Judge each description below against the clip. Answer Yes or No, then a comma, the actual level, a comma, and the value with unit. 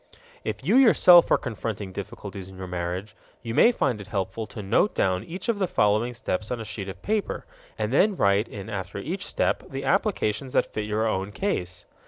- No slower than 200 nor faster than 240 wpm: Yes, fast, 205 wpm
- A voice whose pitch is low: Yes, low, 105 Hz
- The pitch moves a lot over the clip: Yes, wide, 6.0 semitones